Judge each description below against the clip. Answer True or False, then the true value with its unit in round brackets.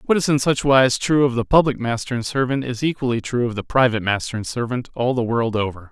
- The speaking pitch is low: True (125 Hz)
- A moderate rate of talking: False (255 wpm)